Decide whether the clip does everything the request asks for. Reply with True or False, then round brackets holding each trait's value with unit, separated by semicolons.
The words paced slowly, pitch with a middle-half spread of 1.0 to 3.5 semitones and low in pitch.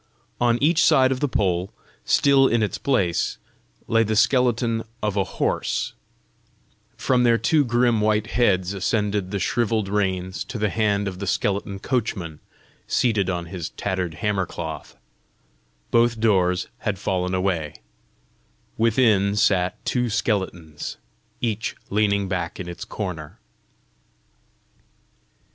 False (125 wpm; 4.0 semitones; 105 Hz)